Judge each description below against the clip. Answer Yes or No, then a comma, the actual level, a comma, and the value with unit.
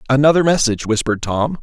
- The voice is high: No, low, 130 Hz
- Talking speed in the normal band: Yes, average, 150 wpm